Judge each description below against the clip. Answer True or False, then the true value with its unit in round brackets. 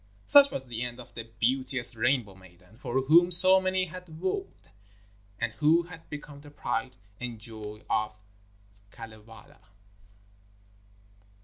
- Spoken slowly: True (130 wpm)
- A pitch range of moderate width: False (6.4 semitones)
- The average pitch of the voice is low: True (130 Hz)